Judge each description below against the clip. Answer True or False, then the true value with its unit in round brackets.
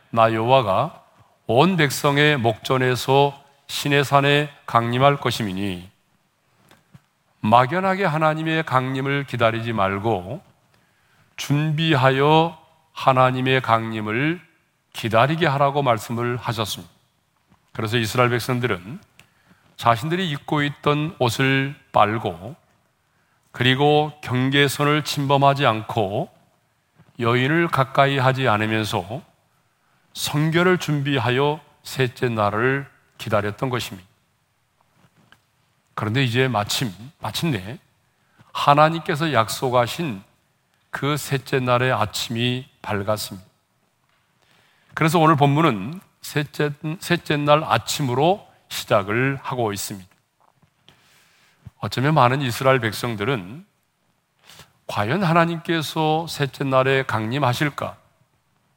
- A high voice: False (135 Hz)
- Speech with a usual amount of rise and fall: True (4.1 semitones)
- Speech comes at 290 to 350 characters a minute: False (225 characters per minute)